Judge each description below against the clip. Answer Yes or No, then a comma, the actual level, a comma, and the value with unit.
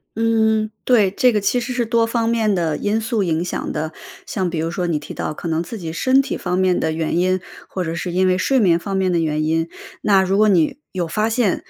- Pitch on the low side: No, medium, 185 Hz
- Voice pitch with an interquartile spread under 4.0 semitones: No, average, 4.7 semitones